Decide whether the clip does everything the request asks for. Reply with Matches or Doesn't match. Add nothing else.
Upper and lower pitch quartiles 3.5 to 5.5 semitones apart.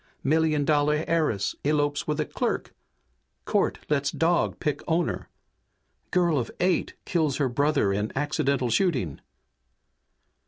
Doesn't match